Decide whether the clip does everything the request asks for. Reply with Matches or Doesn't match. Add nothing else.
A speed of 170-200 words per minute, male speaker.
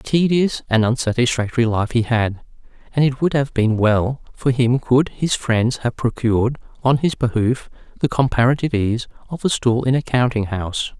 Matches